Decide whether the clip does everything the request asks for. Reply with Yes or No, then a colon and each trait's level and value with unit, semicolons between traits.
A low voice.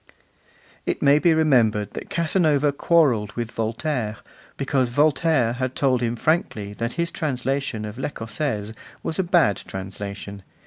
Yes: low, 130 Hz